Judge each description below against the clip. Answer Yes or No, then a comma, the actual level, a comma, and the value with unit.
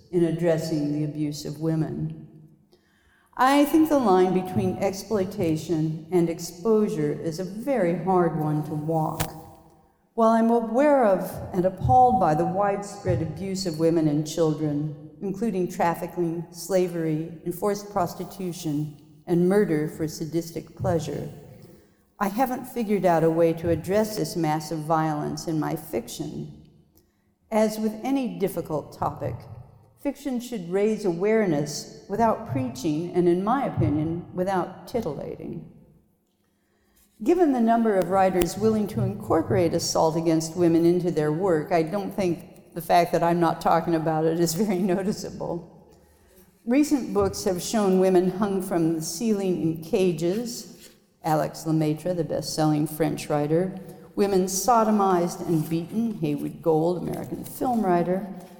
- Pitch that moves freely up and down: No, average, 3.5 semitones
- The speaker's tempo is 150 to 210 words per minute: No, slow, 135 wpm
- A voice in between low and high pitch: Yes, medium, 175 Hz